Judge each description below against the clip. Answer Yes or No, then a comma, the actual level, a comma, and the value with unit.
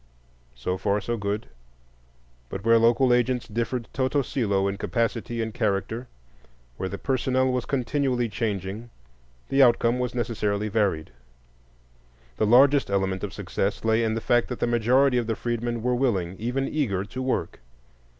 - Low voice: Yes, low, 115 Hz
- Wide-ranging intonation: No, average, 3.4 semitones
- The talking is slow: No, average, 155 wpm